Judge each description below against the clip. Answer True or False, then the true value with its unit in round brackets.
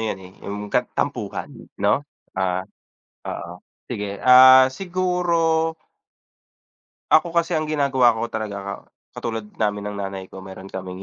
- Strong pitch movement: True (6.1 semitones)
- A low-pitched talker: True (110 Hz)